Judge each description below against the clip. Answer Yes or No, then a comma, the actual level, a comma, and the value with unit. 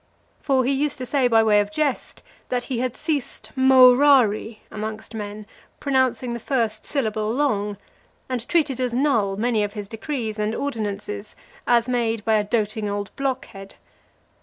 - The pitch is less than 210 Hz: No, high, 230 Hz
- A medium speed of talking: Yes, average, 160 wpm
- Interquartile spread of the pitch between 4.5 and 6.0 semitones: No, average, 3.6 semitones